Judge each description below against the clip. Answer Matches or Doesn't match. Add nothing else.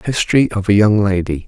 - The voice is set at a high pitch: Doesn't match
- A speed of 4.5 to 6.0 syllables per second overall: Matches